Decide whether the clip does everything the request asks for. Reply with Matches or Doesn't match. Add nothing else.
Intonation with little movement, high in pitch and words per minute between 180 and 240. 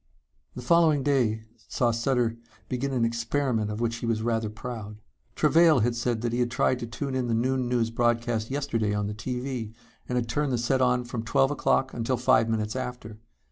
Doesn't match